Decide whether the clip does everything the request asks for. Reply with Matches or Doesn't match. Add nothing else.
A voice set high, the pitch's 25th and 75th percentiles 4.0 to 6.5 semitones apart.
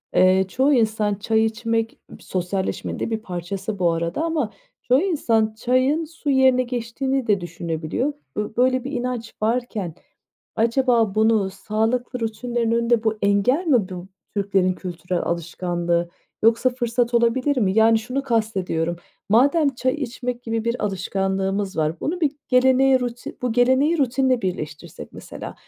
Matches